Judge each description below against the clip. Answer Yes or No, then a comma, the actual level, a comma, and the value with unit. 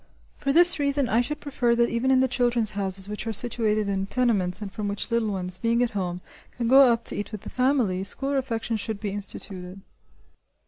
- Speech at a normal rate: No, fast, 215 wpm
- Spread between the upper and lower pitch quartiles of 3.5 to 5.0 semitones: Yes, average, 4.0 semitones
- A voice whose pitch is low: No, high, 230 Hz